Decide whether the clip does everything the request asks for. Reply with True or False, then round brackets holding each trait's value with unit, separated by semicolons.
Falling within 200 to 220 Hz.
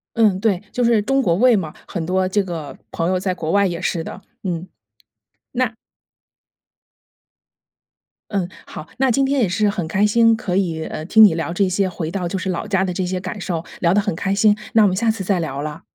False (190 Hz)